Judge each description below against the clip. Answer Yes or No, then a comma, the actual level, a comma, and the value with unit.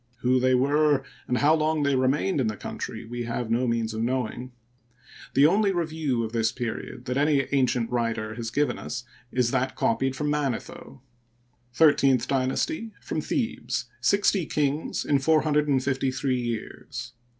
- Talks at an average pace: Yes, average, 155 wpm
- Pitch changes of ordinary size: Yes, average, 3.4 semitones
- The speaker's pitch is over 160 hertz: No, low, 130 Hz